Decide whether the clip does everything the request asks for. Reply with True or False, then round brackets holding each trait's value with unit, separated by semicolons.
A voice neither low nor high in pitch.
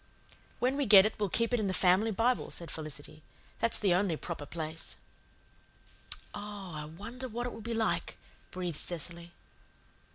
False (195 Hz)